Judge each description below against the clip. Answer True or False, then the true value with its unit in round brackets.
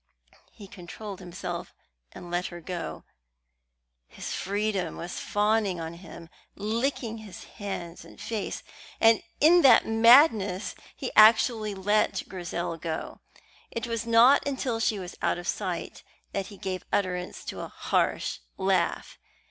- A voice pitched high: True (205 Hz)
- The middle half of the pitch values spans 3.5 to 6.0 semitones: True (4.0 semitones)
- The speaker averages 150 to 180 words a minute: False (135 wpm)